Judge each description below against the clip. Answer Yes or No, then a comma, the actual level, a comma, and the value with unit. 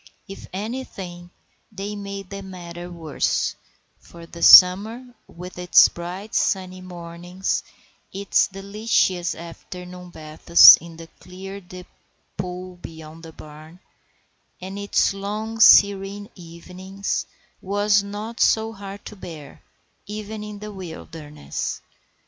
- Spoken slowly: Yes, slow, 115 wpm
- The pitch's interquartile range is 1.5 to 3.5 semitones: Yes, average, 2.7 semitones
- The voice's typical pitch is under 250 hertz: Yes, medium, 185 Hz